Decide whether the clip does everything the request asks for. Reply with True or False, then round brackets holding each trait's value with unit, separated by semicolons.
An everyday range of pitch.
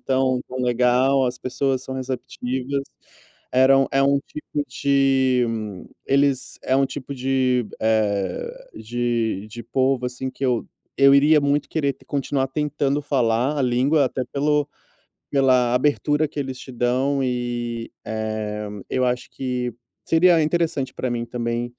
False (2.3 semitones)